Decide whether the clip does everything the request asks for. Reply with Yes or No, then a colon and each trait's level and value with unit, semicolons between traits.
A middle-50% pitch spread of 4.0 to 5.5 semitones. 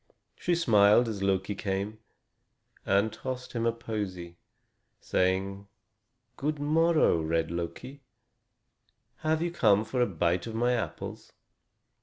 Yes: average, 4.9 semitones